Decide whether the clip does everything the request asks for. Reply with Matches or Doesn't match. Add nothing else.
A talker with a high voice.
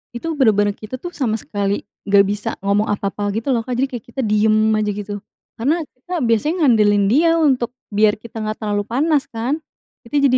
Matches